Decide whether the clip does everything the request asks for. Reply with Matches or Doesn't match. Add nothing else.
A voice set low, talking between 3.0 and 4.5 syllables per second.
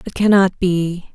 Doesn't match